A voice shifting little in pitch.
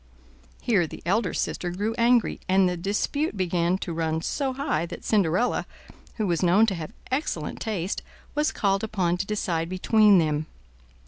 No: average, 4.3 semitones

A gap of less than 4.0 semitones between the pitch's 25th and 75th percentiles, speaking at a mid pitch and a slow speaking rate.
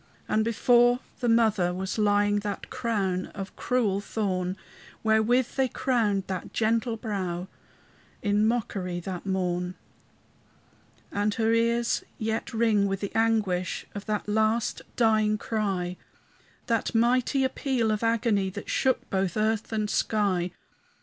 No: average, 2.9 semitones; high, 215 Hz; slow, 130 wpm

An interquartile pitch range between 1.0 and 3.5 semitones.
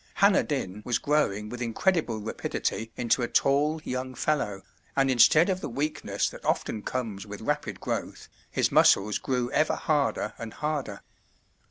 No: average, 5.3 semitones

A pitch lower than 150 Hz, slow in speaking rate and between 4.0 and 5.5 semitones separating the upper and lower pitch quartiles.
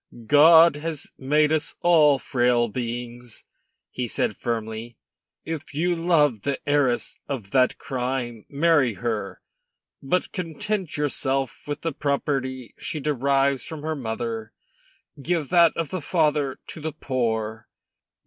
Yes: medium, 140 Hz; slow, 130 wpm; average, 4.4 semitones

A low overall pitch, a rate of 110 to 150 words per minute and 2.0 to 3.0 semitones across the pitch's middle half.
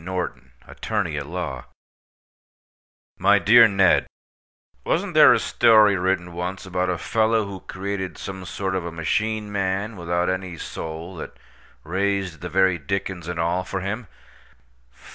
Yes: very low, 95 Hz; average, 140 wpm; narrow, 2.4 semitones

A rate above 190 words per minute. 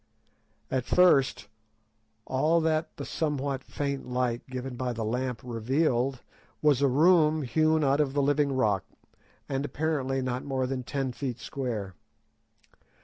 No: average, 140 wpm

